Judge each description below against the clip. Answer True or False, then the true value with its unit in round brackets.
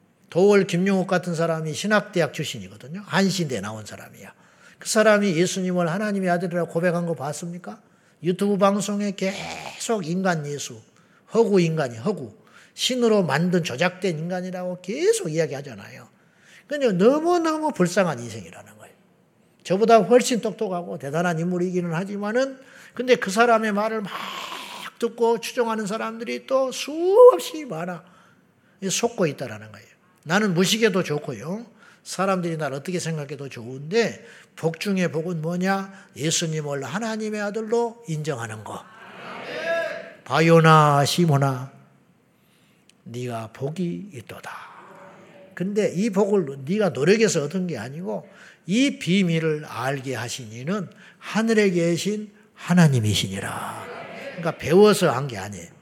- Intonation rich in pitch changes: False (4.8 semitones)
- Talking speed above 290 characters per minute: True (300 characters per minute)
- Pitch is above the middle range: False (180 Hz)